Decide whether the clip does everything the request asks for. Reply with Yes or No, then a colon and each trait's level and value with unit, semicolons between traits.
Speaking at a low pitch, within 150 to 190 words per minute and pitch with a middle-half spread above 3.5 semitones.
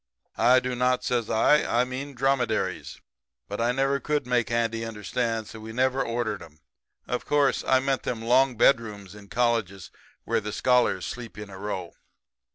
No: low, 120 Hz; average, 170 wpm; average, 2.8 semitones